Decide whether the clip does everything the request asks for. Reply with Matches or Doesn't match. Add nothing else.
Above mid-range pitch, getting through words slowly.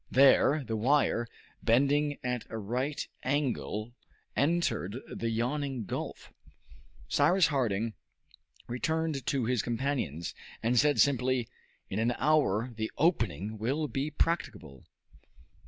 Doesn't match